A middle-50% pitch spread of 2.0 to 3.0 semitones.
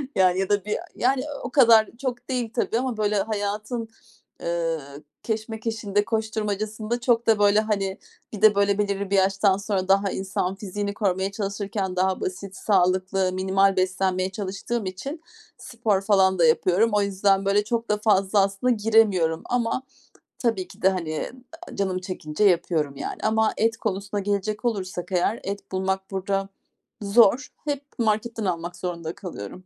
Yes: narrow, 2.6 semitones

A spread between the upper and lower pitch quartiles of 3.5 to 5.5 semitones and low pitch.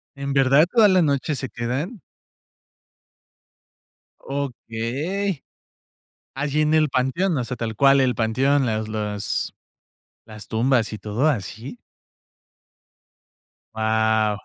Yes: average, 4.8 semitones; low, 130 Hz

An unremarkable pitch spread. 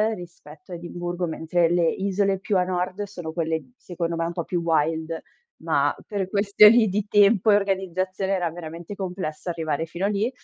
Yes: average, 3.0 semitones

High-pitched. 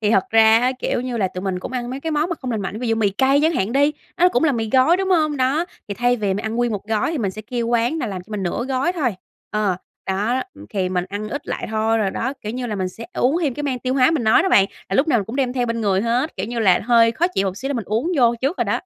Yes: high, 235 Hz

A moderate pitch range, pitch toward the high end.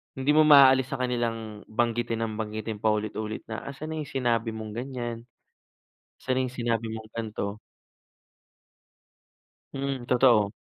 No: average, 3.0 semitones; low, 115 Hz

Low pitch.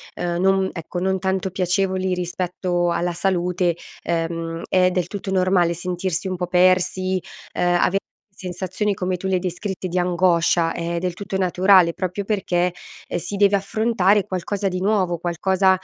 No: medium, 185 Hz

